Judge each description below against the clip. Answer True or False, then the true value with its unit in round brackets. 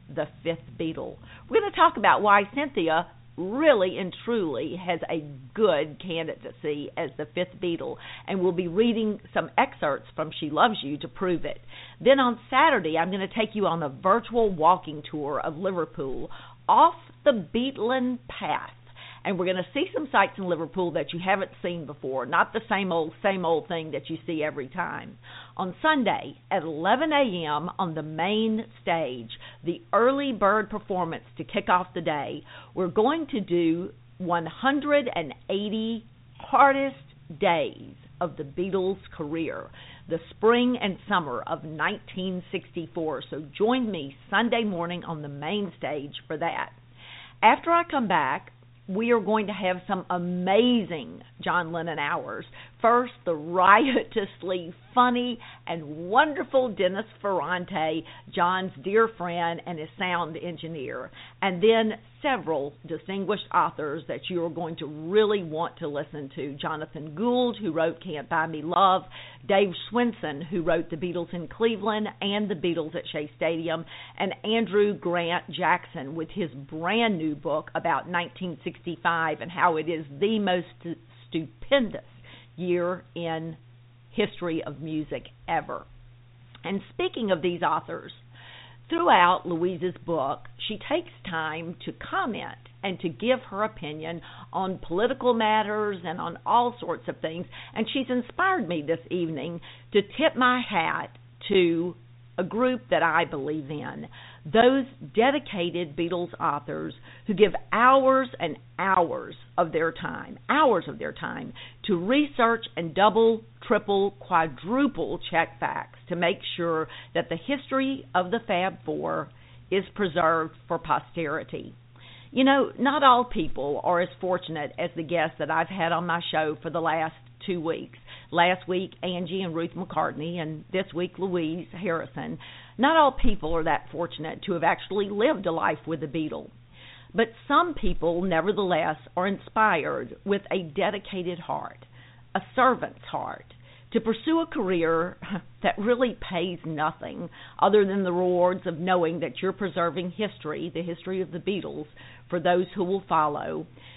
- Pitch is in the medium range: True (175 Hz)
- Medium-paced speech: True (150 wpm)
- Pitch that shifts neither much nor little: True (4.6 semitones)